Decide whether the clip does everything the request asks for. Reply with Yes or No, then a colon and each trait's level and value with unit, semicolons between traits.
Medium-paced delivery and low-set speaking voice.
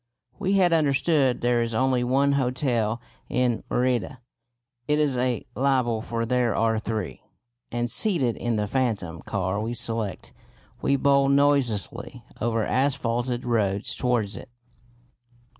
No: slow, 130 wpm; low, 125 Hz